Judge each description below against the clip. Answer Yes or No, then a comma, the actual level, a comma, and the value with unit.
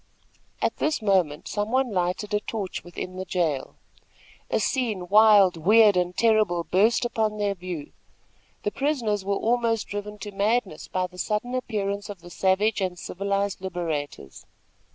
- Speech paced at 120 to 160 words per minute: Yes, average, 155 wpm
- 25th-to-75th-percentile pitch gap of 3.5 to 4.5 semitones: No, average, 3.1 semitones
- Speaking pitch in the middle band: No, high, 200 Hz